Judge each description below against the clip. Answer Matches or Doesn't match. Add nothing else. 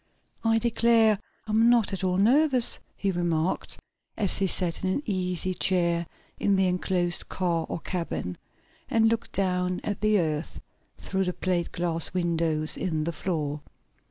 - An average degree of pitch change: Matches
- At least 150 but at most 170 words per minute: Matches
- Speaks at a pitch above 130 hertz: Matches